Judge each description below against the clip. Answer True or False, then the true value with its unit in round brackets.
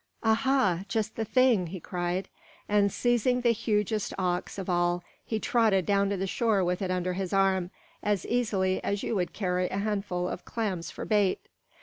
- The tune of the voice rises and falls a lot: False (3.2 semitones)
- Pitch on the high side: True (195 Hz)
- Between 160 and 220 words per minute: True (185 wpm)